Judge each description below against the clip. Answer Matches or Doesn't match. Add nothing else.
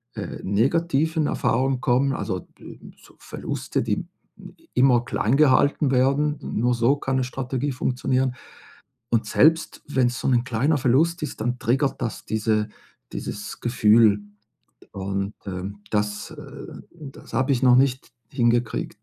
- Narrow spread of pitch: Doesn't match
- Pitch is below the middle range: Matches